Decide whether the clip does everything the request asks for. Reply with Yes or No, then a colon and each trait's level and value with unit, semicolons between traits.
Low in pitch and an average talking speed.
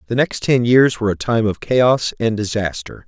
No: low, 110 Hz; fast, 215 wpm